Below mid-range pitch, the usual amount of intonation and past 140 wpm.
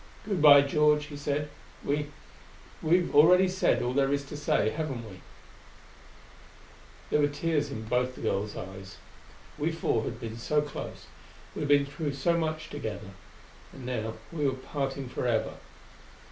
No: medium, 145 Hz; average, 3.6 semitones; average, 160 wpm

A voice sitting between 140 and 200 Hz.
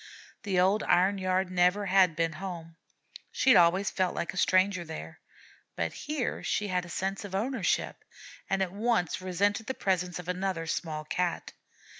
Yes: medium, 185 Hz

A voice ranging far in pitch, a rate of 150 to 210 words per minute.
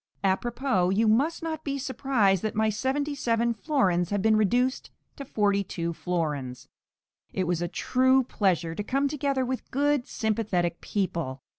Yes: wide, 6.4 semitones; average, 160 wpm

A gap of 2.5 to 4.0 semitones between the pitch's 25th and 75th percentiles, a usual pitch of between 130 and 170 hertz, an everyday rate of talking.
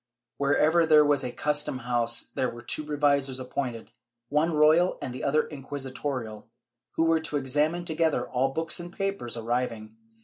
Yes: average, 3.7 semitones; medium, 140 Hz; average, 160 wpm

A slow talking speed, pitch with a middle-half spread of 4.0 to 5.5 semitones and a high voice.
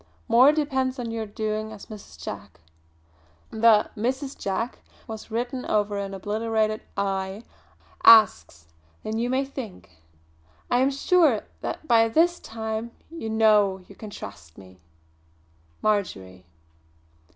No: slow, 125 wpm; average, 3.4 semitones; high, 220 Hz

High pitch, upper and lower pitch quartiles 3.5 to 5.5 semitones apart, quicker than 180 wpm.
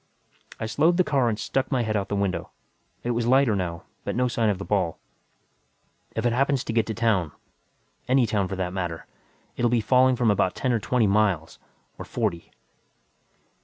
No: low, 110 Hz; average, 4.2 semitones; average, 195 wpm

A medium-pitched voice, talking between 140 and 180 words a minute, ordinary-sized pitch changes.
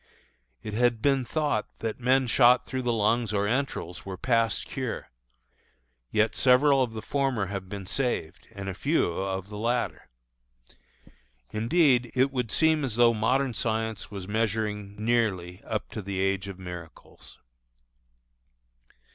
No: low, 110 Hz; average, 145 wpm; average, 4.0 semitones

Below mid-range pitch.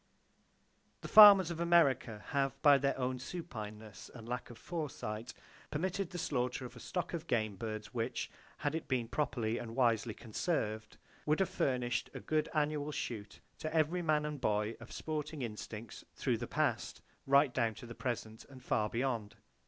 Yes: low, 125 Hz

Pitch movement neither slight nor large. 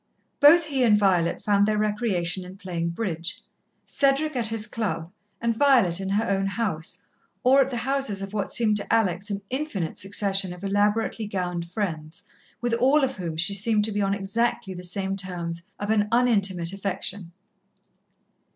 Yes: average, 3.8 semitones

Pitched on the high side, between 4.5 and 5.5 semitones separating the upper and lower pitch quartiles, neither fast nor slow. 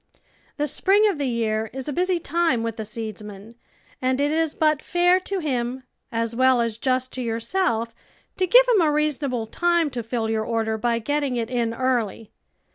Yes: very high, 255 Hz; average, 5.2 semitones; average, 190 wpm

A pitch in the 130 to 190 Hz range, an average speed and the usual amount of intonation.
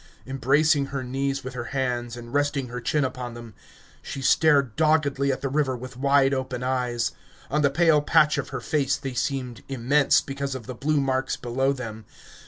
No: low, 135 Hz; average, 190 wpm; narrow, 2.1 semitones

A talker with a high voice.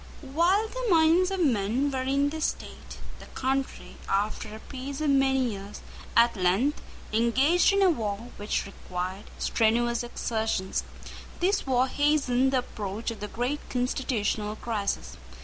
Yes: very high, 250 Hz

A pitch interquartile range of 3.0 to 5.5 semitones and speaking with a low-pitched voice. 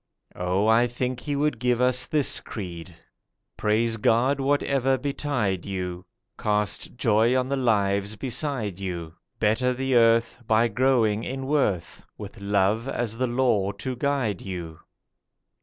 Yes: average, 4.5 semitones; low, 115 Hz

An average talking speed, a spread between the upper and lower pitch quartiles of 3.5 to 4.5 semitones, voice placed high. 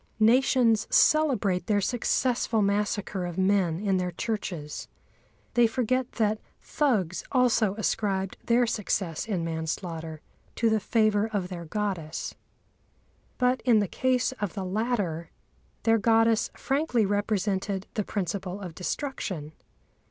No: slow, 120 wpm; average, 3.8 semitones; high, 205 Hz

